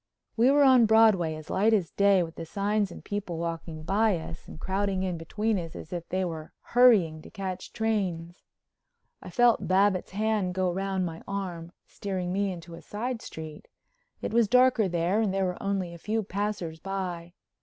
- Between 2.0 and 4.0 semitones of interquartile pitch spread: Yes, average, 3.6 semitones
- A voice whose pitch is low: No, high, 190 Hz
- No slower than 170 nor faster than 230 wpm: Yes, average, 185 wpm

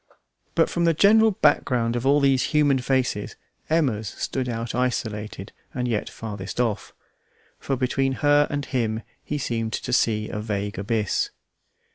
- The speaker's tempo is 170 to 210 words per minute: No, average, 150 wpm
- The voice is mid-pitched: No, low, 125 Hz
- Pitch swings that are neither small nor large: Yes, average, 4.2 semitones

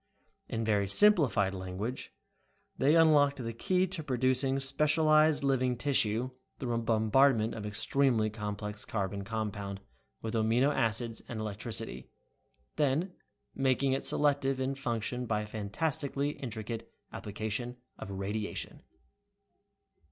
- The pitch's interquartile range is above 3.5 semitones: Yes, average, 4.2 semitones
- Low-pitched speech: Yes, low, 120 Hz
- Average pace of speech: No, slow, 120 wpm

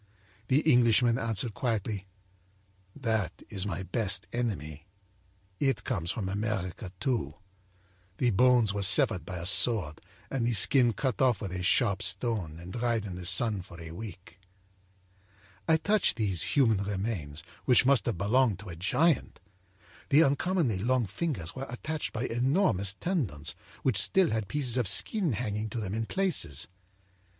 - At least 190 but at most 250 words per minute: No, average, 155 wpm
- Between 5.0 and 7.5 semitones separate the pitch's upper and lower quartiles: Yes, average, 5.3 semitones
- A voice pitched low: Yes, low, 110 Hz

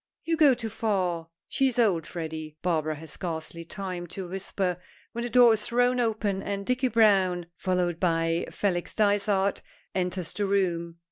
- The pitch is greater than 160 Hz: Yes, high, 190 Hz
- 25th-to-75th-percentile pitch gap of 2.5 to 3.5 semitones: No, average, 4.2 semitones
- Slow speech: No, average, 160 wpm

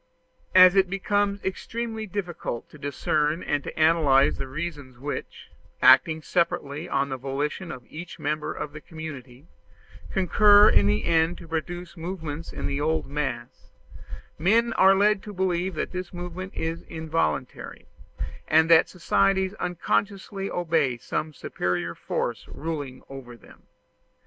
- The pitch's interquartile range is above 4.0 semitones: Yes, average, 4.6 semitones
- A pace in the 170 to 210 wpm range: No, average, 140 wpm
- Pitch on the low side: No, medium, 160 Hz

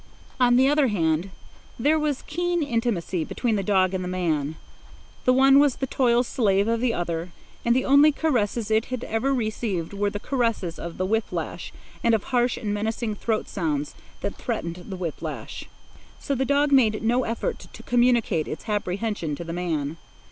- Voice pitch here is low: No, high, 220 Hz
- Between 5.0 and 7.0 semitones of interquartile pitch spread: Yes, wide, 5.6 semitones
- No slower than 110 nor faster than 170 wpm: No, average, 185 wpm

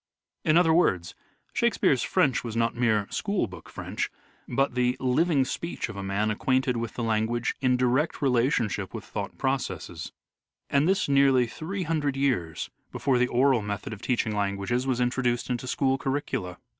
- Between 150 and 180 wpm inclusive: Yes, average, 165 wpm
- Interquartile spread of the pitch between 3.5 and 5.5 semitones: Yes, average, 3.9 semitones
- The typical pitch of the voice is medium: No, low, 125 Hz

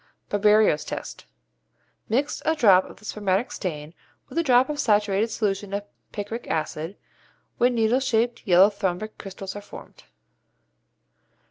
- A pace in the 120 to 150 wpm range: Yes, average, 140 wpm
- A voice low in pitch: No, high, 210 Hz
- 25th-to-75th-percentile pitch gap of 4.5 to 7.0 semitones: No, average, 3.4 semitones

